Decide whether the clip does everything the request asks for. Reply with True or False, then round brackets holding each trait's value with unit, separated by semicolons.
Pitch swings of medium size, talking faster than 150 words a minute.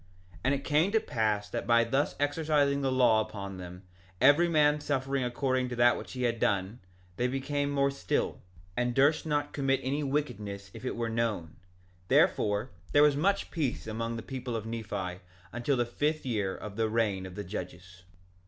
True (5.0 semitones; 190 wpm)